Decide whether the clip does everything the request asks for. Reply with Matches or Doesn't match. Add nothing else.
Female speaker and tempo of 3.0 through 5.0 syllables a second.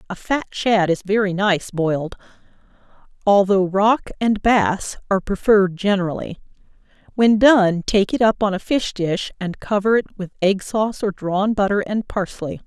Matches